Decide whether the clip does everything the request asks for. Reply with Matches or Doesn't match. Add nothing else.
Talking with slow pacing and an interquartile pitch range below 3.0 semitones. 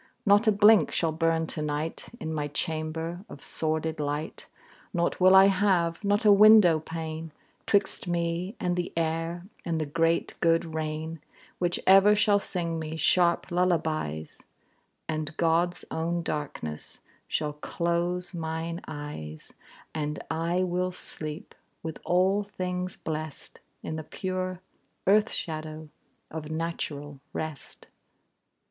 Matches